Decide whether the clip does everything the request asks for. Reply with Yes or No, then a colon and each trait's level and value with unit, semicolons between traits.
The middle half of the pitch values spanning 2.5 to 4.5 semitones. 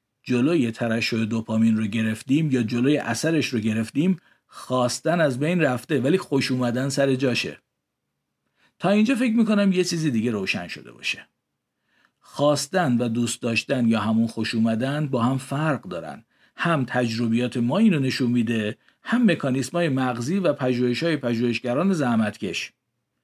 No: average, 4.9 semitones